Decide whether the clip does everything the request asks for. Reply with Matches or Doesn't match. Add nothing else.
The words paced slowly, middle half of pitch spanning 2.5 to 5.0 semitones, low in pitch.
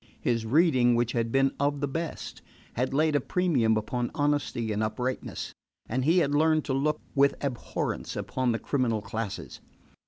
Doesn't match